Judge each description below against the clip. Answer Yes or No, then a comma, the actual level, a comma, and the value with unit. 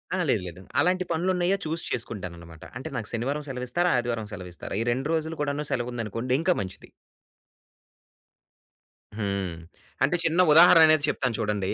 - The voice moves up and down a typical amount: No, wide, 7.4 semitones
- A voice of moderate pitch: No, low, 125 Hz